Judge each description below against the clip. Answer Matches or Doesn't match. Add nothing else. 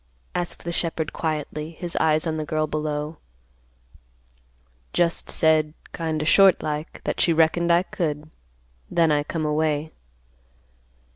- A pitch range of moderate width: Doesn't match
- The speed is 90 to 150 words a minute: Matches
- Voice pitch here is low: Doesn't match